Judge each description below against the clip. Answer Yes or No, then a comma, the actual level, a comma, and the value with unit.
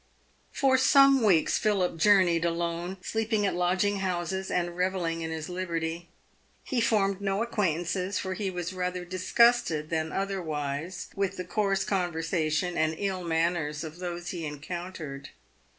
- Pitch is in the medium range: Yes, medium, 180 Hz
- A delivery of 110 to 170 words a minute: Yes, average, 140 wpm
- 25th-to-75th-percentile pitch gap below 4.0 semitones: Yes, average, 2.8 semitones